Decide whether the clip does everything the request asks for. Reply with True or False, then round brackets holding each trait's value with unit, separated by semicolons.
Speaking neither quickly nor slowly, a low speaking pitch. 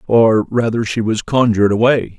True (165 wpm; 110 Hz)